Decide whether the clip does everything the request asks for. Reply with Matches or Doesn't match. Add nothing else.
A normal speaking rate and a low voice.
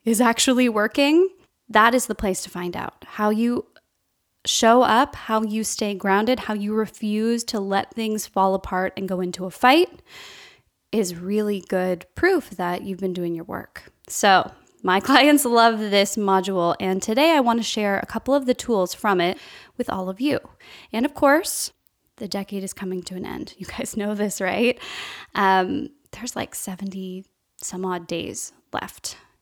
Doesn't match